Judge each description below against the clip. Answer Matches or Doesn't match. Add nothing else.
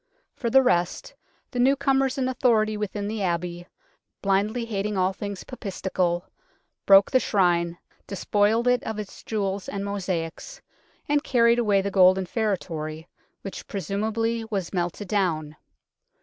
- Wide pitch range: Doesn't match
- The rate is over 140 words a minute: Doesn't match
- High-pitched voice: Matches